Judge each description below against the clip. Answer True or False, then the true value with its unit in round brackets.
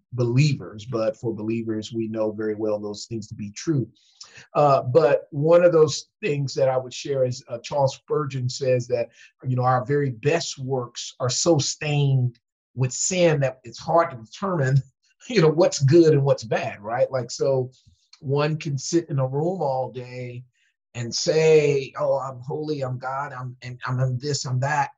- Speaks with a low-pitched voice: True (130 Hz)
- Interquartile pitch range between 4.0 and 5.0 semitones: False (3.2 semitones)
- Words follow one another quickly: False (185 wpm)